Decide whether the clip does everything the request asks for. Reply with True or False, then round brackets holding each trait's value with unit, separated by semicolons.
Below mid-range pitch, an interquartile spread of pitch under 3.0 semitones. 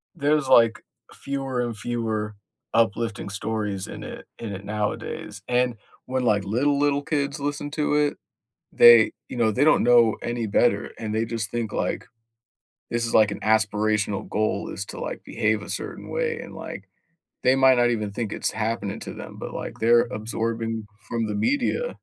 False (115 Hz; 3.3 semitones)